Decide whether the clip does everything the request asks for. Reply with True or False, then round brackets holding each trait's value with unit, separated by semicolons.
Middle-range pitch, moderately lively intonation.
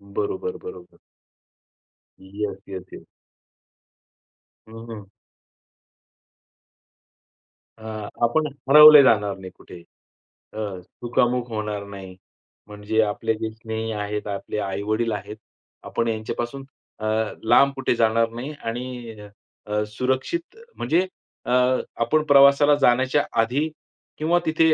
False (115 Hz; 3.9 semitones)